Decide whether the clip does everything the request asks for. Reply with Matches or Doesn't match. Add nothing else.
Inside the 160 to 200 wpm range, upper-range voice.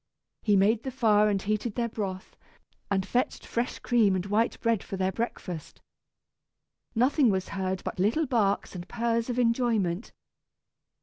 Doesn't match